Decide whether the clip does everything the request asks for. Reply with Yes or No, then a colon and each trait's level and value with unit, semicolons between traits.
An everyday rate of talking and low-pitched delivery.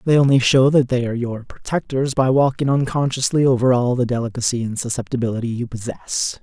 Yes: average, 175 wpm; low, 125 Hz